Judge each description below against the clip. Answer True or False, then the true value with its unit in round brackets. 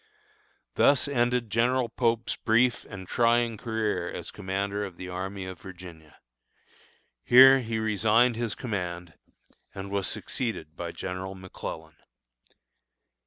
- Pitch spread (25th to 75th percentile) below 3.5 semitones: False (4.1 semitones)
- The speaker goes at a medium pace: False (120 wpm)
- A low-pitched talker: True (105 Hz)